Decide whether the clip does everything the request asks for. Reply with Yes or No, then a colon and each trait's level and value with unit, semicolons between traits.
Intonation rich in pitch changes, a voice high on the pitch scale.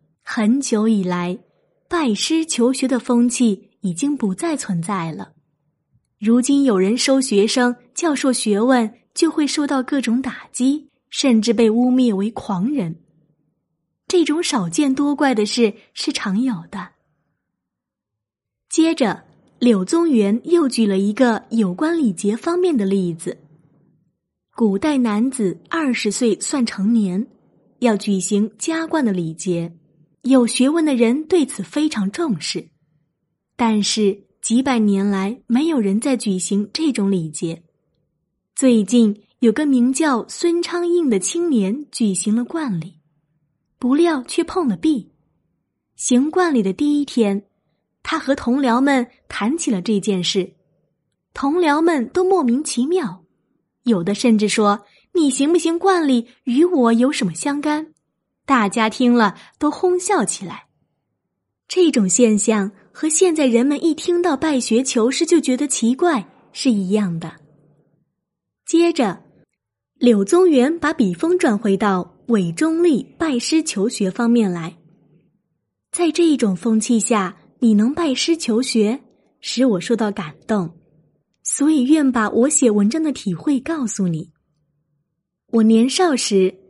Yes: wide, 6.4 semitones; high, 235 Hz